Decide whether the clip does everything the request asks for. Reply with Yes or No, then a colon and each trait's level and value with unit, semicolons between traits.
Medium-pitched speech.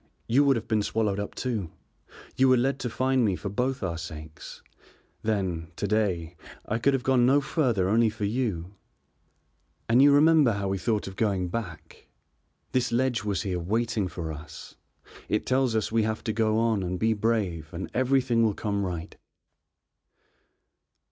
No: low, 110 Hz